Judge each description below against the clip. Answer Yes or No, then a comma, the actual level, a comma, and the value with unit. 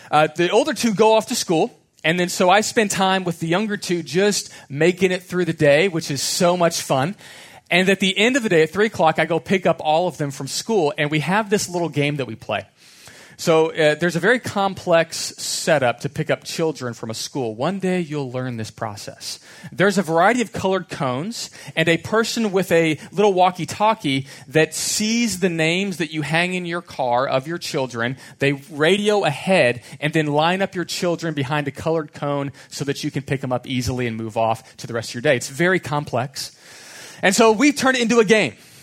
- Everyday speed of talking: No, fast, 225 wpm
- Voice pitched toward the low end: No, medium, 165 Hz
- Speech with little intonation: No, average, 5.2 semitones